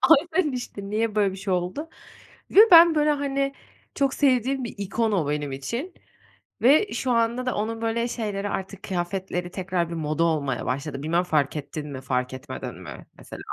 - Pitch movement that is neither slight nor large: No, wide, 7.6 semitones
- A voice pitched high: Yes, high, 200 Hz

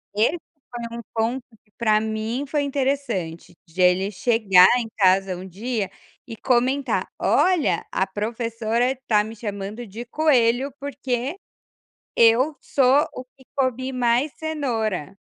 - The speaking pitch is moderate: No, high, 235 Hz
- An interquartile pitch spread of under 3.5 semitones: No, average, 3.9 semitones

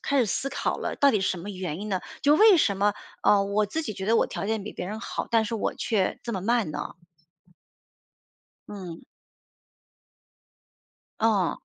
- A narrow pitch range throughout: No, average, 3.2 semitones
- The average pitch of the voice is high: Yes, high, 205 Hz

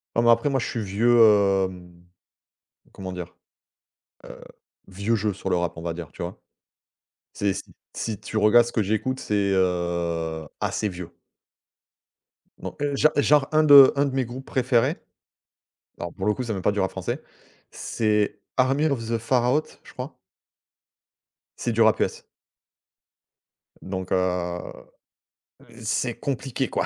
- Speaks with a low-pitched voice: Yes, low, 110 Hz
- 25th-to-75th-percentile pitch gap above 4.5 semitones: Yes, wide, 5.5 semitones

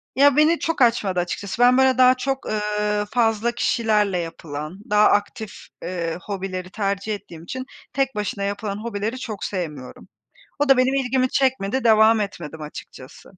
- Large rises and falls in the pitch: No, average, 4.6 semitones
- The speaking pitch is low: No, high, 210 Hz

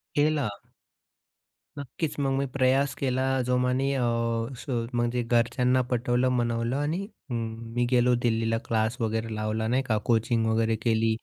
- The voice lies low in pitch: Yes, low, 120 Hz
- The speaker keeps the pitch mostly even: Yes, narrow, 2.3 semitones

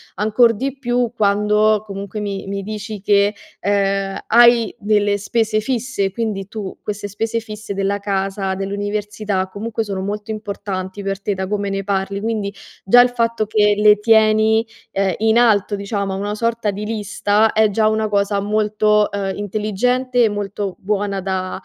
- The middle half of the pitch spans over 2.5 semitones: No, narrow, 1.6 semitones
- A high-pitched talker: Yes, high, 210 Hz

